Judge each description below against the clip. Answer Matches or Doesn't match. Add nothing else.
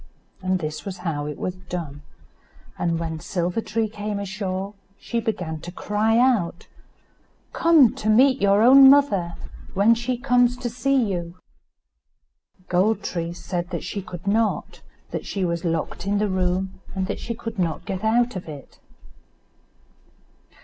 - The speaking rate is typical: Matches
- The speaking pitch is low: Doesn't match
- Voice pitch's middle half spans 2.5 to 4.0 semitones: Doesn't match